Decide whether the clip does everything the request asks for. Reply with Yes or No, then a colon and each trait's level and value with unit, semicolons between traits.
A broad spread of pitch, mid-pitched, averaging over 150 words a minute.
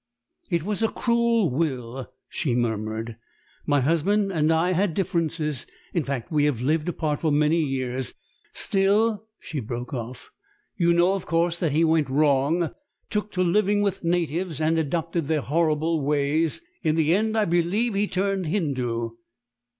No: average, 4.5 semitones; medium, 160 Hz; average, 160 wpm